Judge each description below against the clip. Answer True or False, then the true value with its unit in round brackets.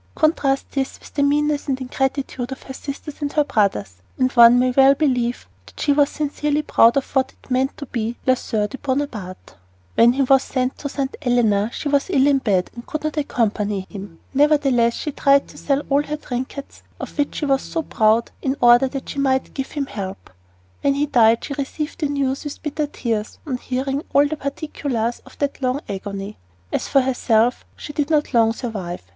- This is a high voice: True (265 Hz)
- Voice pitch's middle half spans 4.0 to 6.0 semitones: False (3.4 semitones)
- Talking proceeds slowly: False (205 wpm)